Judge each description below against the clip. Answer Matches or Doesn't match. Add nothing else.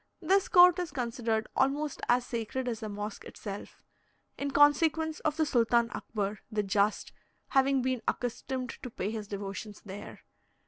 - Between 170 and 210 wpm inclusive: Doesn't match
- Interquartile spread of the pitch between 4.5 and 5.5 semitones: Matches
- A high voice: Matches